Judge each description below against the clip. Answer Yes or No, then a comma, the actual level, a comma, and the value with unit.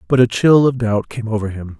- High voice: No, low, 115 Hz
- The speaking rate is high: Yes, fast, 265 wpm